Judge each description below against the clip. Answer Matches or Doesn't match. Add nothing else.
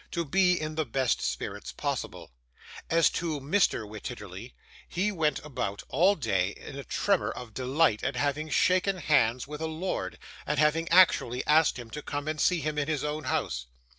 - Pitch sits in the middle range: Matches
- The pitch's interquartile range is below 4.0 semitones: Doesn't match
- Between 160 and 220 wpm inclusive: Matches